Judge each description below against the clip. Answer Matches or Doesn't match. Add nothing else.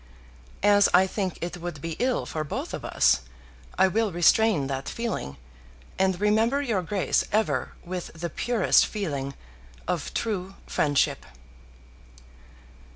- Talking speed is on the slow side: Matches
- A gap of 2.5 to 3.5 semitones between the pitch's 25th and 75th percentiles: Doesn't match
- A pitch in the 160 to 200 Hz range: Matches